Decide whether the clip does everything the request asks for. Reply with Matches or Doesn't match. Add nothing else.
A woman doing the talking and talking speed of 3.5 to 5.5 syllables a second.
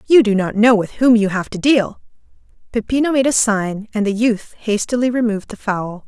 Matches